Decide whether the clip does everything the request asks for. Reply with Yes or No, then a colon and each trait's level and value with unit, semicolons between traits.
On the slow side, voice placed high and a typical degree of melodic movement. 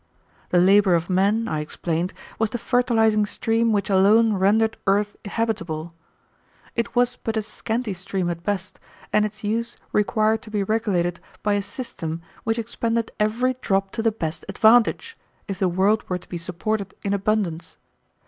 No: average, 165 wpm; high, 210 Hz; average, 3.0 semitones